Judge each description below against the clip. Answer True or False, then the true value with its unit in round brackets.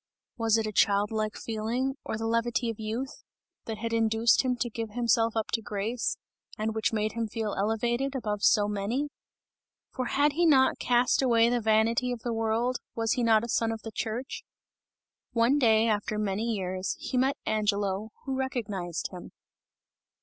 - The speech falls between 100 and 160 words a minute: False (175 wpm)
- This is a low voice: False (225 Hz)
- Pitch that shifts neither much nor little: False (2.1 semitones)